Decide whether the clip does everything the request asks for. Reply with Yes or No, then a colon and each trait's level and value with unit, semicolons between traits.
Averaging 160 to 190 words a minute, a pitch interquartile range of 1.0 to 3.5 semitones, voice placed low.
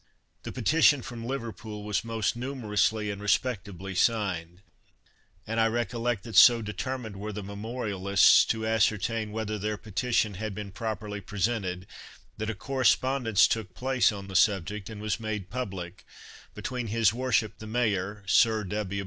No: average, 150 wpm; narrow, 2.5 semitones; low, 110 Hz